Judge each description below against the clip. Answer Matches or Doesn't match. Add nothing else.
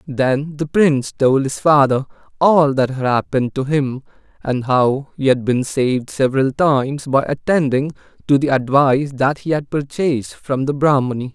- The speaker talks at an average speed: Matches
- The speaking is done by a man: Matches